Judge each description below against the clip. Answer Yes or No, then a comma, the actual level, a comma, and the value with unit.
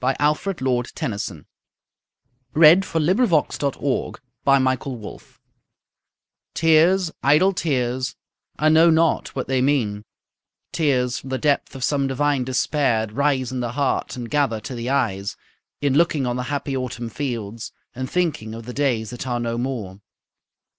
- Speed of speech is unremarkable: Yes, average, 160 wpm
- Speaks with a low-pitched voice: Yes, low, 130 Hz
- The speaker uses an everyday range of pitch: Yes, average, 3.4 semitones